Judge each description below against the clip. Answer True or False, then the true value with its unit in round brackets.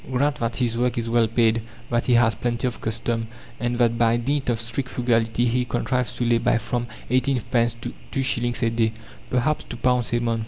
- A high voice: False (120 Hz)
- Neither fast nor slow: False (220 wpm)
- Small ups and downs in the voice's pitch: True (1.4 semitones)